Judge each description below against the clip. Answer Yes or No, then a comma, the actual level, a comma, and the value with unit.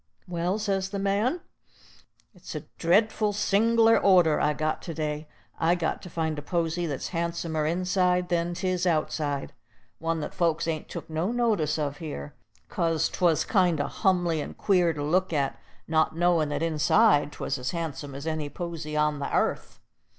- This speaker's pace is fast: No, average, 170 wpm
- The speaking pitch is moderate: Yes, medium, 165 Hz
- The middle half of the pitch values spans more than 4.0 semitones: No, average, 3.1 semitones